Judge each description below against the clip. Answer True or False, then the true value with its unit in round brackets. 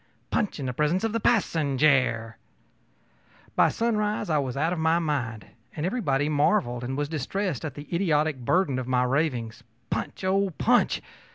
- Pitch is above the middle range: False (150 Hz)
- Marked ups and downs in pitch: True (6.0 semitones)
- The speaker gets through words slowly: False (165 wpm)